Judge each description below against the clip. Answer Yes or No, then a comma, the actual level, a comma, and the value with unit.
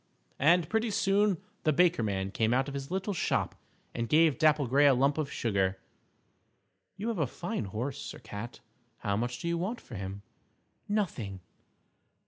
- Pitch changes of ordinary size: No, wide, 7.6 semitones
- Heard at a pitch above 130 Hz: Yes, medium, 140 Hz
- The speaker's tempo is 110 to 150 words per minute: No, average, 170 wpm